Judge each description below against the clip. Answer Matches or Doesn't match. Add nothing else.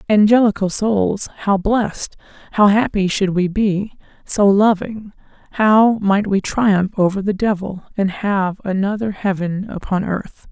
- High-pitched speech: Matches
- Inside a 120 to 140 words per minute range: Matches